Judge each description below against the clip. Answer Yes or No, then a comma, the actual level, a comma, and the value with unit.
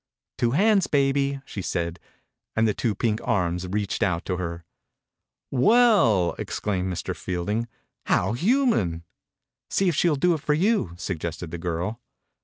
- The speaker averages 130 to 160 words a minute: No, average, 175 wpm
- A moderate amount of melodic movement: No, wide, 8.9 semitones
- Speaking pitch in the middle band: No, low, 105 Hz